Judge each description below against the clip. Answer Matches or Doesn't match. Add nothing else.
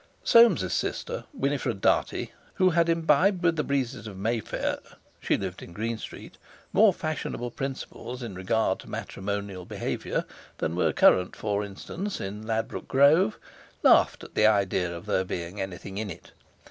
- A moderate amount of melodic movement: Doesn't match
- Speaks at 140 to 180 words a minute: Matches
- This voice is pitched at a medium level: Doesn't match